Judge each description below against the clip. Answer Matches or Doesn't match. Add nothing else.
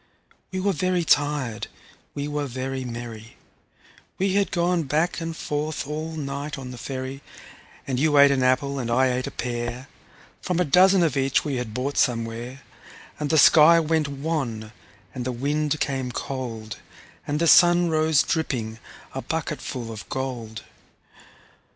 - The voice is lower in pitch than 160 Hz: Matches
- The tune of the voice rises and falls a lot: Doesn't match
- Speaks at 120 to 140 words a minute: Doesn't match